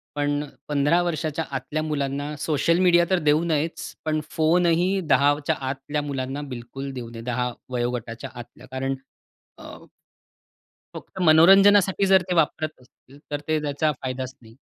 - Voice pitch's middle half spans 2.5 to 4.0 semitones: Yes, average, 3.6 semitones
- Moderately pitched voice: Yes, medium, 145 Hz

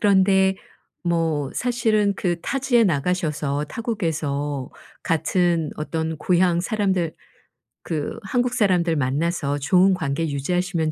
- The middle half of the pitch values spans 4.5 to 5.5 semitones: No, average, 4.1 semitones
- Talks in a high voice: No, medium, 175 Hz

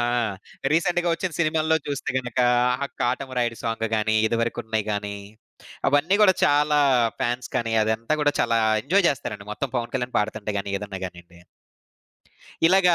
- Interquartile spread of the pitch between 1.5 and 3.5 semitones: No, wide, 5.4 semitones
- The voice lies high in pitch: No, low, 120 Hz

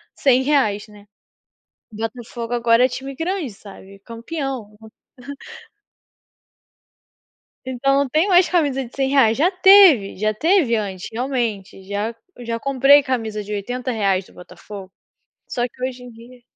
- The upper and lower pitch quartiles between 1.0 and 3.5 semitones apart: No, average, 4.3 semitones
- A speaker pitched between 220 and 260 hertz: Yes, high, 245 Hz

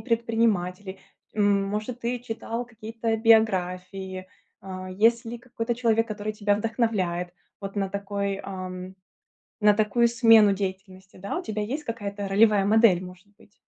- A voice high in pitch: Yes, high, 210 Hz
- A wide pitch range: No, average, 2.9 semitones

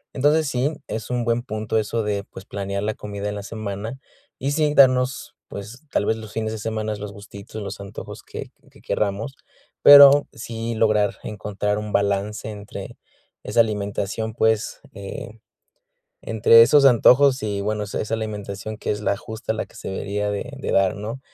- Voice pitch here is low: Yes, low, 110 Hz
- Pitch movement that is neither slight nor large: No, narrow, 2.2 semitones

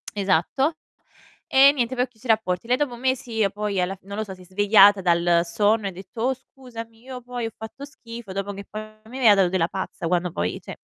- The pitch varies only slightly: No, average, 4.4 semitones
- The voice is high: Yes, high, 215 Hz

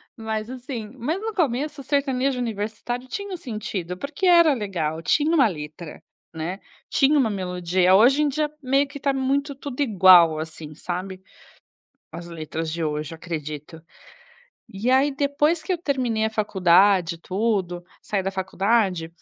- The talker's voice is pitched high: Yes, high, 215 Hz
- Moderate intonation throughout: No, wide, 7.7 semitones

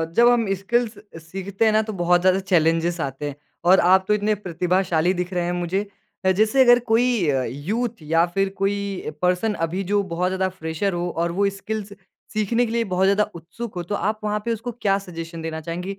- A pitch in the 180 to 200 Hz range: Yes, high, 190 Hz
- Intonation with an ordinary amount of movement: Yes, average, 3.6 semitones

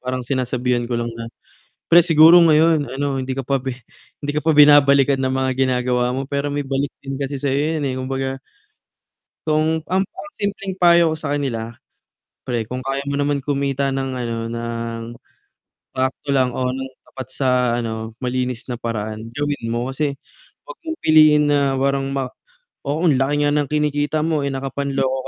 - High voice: No, low, 135 Hz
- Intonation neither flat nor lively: No, narrow, 2.3 semitones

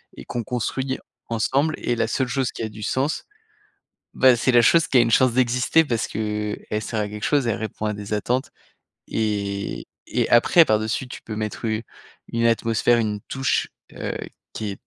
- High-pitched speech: No, low, 115 Hz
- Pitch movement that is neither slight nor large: Yes, average, 3.1 semitones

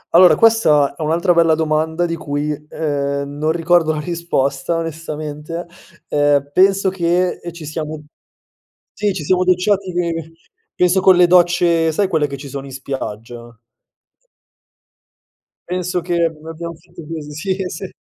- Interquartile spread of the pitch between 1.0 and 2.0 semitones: No, average, 2.8 semitones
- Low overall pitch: No, medium, 165 Hz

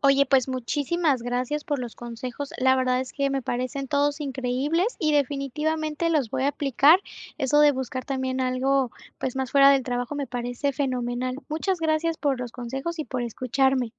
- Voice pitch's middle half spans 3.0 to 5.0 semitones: No, narrow, 2.4 semitones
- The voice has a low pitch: No, very high, 270 Hz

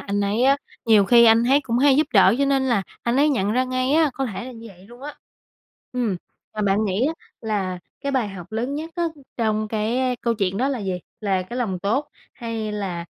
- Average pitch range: Yes, average, 4.3 semitones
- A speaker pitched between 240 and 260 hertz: No, high, 230 Hz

